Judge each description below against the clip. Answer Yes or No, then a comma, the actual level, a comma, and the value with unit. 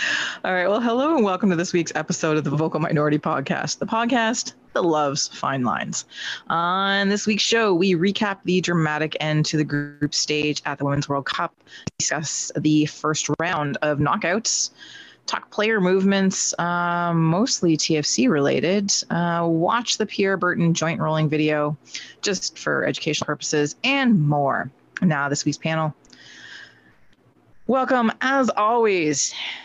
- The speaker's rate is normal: Yes, average, 150 wpm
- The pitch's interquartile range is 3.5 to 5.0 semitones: Yes, average, 4.7 semitones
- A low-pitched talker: No, medium, 170 Hz